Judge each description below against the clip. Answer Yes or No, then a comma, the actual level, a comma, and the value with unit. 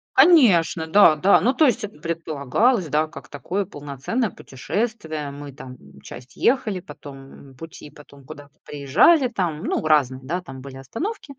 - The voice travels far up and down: Yes, wide, 6.8 semitones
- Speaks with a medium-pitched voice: Yes, medium, 155 Hz